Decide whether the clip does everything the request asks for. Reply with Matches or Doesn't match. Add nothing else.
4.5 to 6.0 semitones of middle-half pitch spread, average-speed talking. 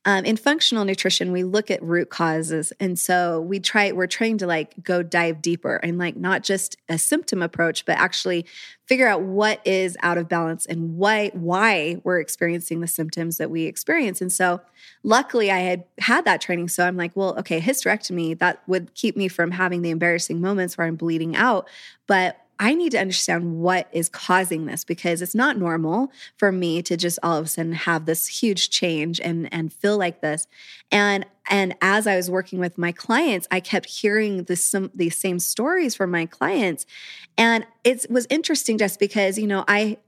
Doesn't match